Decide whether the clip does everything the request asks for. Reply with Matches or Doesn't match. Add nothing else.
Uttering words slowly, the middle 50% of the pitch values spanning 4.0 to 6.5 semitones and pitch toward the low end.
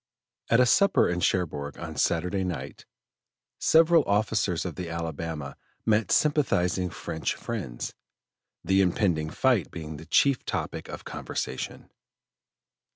Matches